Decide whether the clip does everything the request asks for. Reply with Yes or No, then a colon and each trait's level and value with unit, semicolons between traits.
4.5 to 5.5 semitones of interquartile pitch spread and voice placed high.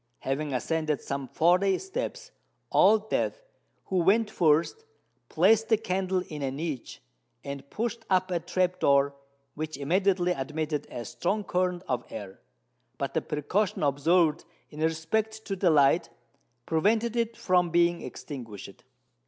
No: average, 5.2 semitones; medium, 175 Hz